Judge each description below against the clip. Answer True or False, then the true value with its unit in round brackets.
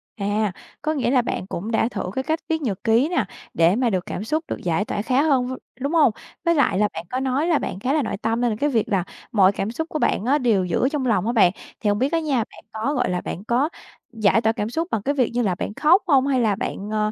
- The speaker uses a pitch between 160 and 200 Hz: False (240 Hz)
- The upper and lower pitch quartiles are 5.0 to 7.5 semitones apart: True (5.3 semitones)